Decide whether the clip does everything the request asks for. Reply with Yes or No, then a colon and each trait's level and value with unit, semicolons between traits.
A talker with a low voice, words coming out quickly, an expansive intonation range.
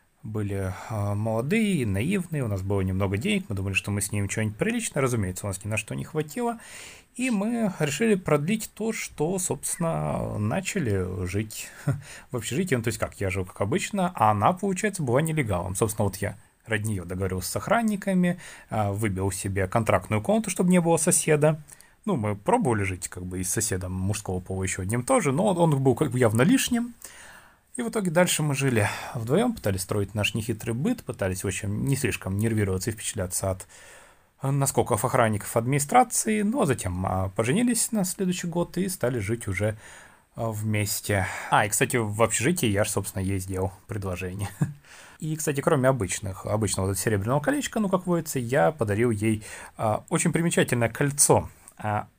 Yes: low, 115 Hz; fast, 170 wpm; wide, 8.6 semitones